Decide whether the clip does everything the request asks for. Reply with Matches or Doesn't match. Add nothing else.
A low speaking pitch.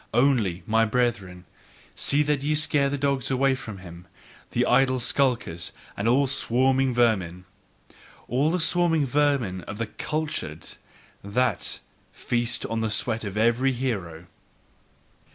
Matches